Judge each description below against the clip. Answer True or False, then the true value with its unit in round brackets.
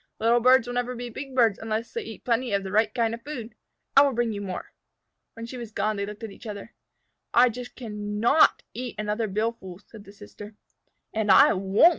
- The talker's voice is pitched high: True (225 Hz)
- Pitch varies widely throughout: False (2.8 semitones)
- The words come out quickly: True (220 wpm)